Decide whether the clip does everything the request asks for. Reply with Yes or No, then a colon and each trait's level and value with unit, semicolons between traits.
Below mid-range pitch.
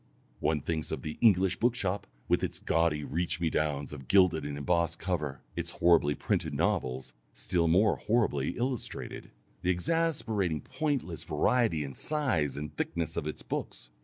Yes: very low, 85 Hz